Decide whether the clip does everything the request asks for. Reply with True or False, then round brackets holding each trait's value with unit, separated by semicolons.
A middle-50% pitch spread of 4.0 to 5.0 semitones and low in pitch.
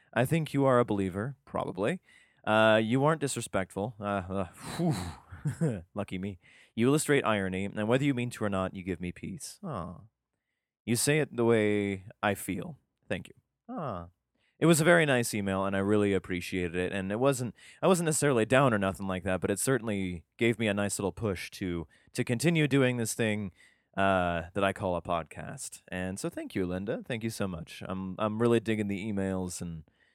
True (4.5 semitones; 105 Hz)